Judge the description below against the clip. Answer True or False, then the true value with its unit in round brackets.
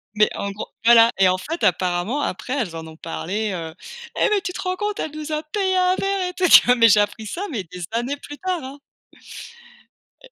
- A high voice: True (245 Hz)